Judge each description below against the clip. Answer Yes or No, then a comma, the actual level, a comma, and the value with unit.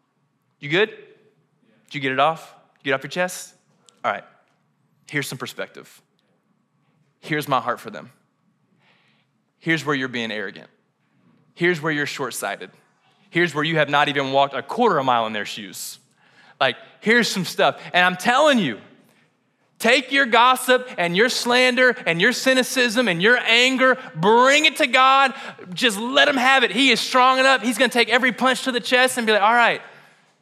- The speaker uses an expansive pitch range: Yes, wide, 8.3 semitones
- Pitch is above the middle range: Yes, high, 230 Hz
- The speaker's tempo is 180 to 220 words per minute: Yes, average, 185 wpm